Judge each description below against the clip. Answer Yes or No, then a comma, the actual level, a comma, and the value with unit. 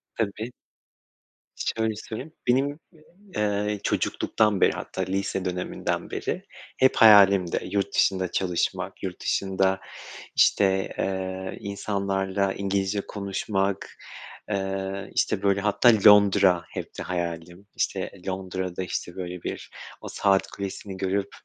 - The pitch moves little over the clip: Yes, narrow, 1.4 semitones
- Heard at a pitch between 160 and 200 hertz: No, very low, 95 Hz